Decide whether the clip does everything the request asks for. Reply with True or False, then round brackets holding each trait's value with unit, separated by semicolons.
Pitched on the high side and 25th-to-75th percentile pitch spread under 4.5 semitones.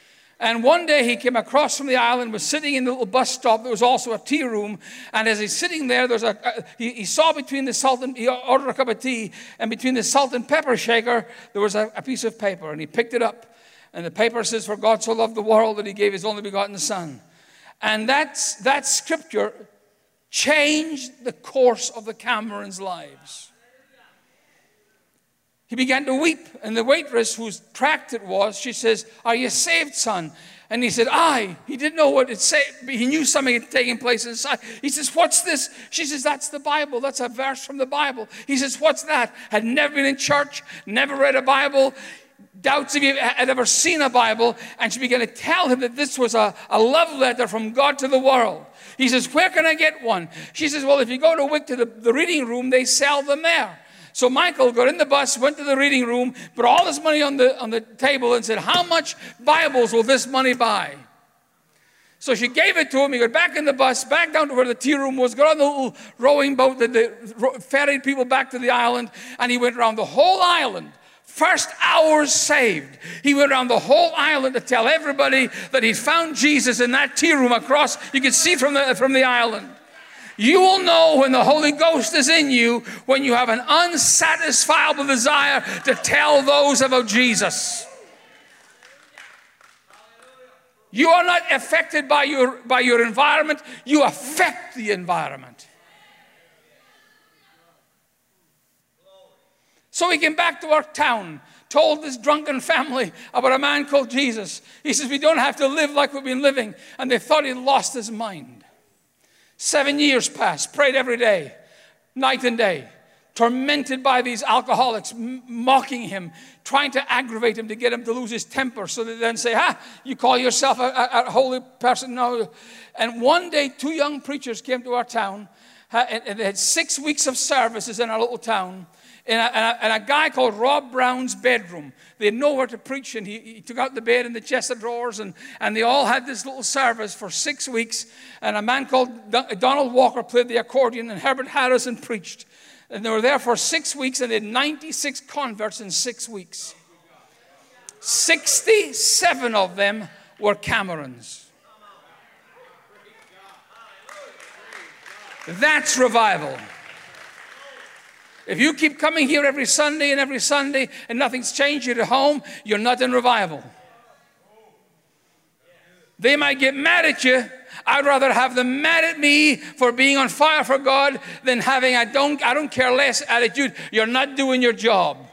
True (255 Hz; 3.5 semitones)